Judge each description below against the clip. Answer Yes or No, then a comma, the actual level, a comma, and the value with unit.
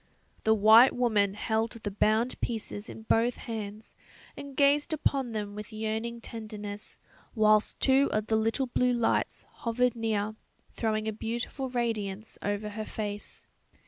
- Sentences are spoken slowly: No, average, 145 wpm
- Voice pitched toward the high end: Yes, high, 220 Hz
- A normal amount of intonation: No, narrow, 2.1 semitones